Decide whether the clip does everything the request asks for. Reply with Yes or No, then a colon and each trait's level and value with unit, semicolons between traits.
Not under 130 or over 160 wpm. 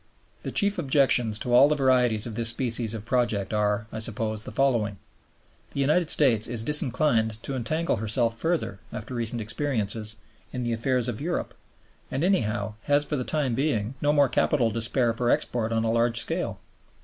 No: average, 185 wpm